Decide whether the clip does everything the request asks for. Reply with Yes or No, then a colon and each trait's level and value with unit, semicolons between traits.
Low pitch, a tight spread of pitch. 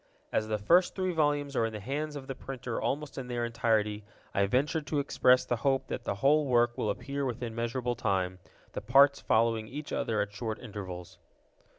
No: low, 120 Hz; average, 4.3 semitones